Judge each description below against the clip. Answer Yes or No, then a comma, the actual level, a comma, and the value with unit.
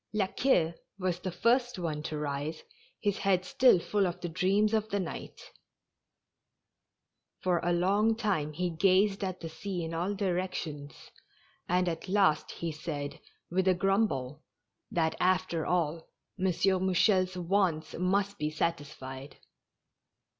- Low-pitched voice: No, medium, 180 Hz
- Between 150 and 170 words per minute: No, average, 140 wpm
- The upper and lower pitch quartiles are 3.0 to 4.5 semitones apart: Yes, average, 3.3 semitones